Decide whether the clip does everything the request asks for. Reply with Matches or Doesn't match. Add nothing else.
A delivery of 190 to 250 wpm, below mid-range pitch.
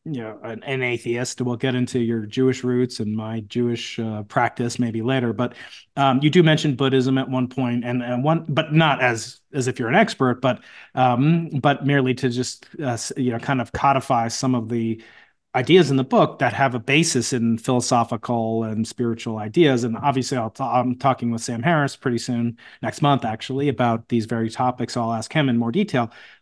Matches